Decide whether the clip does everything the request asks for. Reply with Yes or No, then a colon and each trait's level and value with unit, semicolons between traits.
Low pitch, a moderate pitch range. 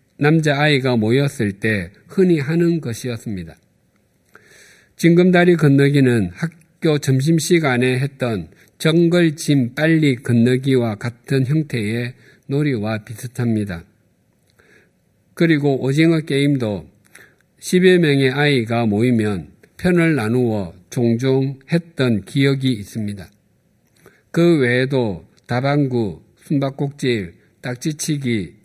Yes: low, 130 Hz; average, 4.8 semitones